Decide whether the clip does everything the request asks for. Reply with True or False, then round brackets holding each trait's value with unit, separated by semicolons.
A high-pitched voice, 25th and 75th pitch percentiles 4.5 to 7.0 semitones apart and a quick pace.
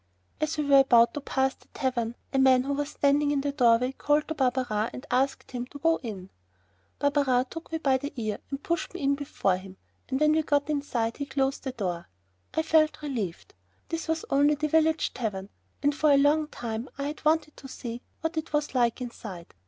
False (275 Hz; 3.6 semitones; 215 wpm)